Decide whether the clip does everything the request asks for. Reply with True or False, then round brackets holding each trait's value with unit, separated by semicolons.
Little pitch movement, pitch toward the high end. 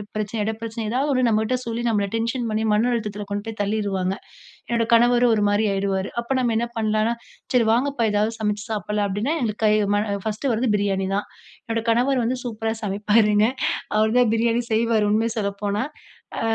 True (2.0 semitones; 220 Hz)